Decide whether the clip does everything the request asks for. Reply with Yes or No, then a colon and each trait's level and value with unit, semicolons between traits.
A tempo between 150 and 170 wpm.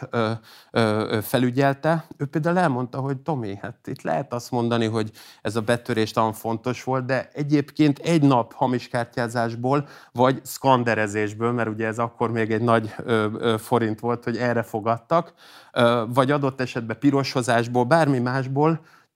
No: average, 140 wpm